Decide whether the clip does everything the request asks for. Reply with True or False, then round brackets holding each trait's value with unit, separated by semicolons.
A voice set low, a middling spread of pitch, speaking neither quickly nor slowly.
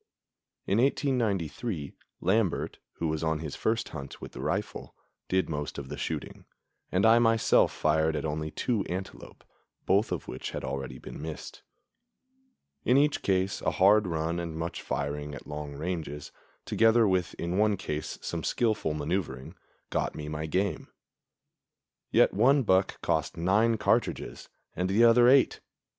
False (90 Hz; 6.1 semitones; 150 wpm)